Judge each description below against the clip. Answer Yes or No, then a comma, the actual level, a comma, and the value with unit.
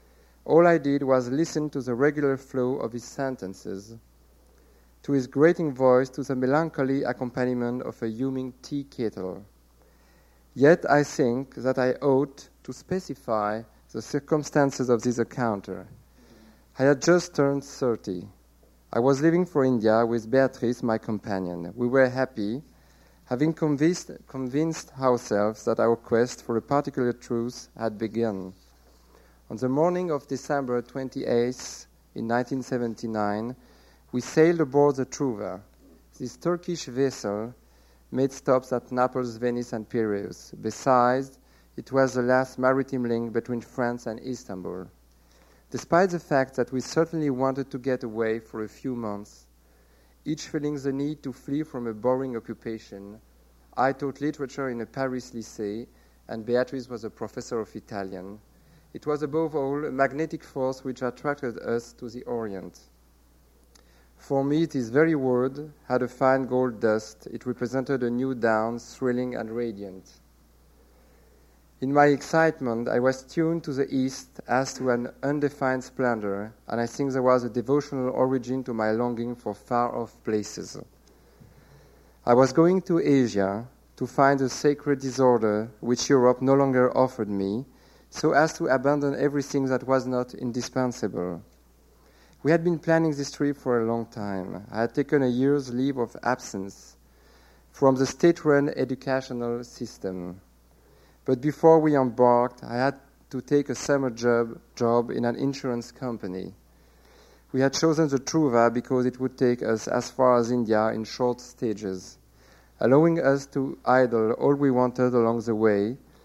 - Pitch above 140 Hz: No, low, 125 Hz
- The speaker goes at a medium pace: Yes, average, 150 wpm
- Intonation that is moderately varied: Yes, average, 3.8 semitones